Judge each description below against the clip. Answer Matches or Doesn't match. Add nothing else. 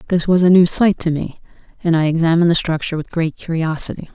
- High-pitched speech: Doesn't match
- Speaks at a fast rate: Matches